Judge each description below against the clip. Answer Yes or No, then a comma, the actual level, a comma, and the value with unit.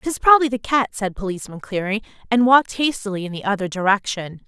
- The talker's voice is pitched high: Yes, high, 215 Hz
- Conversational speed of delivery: Yes, average, 190 wpm